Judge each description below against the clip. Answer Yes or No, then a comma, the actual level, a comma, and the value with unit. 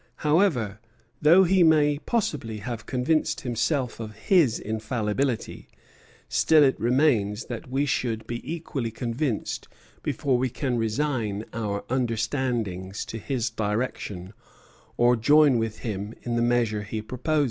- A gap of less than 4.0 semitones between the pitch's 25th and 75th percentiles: No, average, 4.4 semitones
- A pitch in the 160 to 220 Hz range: No, low, 120 Hz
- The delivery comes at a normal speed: No, slow, 130 wpm